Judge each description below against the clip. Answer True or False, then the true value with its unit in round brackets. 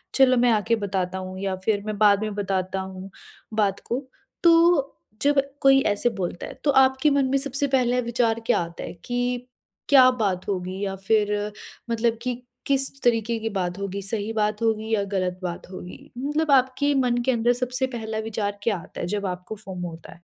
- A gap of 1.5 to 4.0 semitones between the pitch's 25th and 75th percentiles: False (4.6 semitones)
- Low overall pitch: False (220 Hz)